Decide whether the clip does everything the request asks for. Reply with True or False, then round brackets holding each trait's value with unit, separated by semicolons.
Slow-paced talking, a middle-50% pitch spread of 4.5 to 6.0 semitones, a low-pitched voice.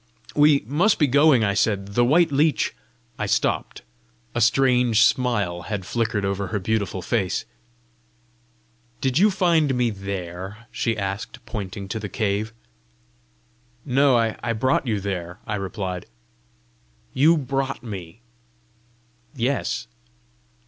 True (125 wpm; 5.1 semitones; 115 Hz)